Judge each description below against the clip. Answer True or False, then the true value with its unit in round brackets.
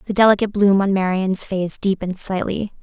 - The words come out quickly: False (170 wpm)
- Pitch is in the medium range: False (195 Hz)